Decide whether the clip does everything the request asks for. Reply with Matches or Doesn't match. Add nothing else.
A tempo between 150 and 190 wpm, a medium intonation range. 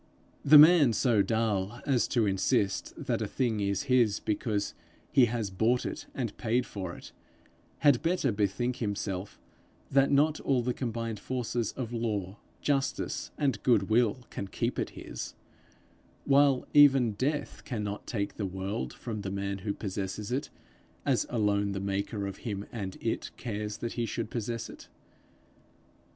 Matches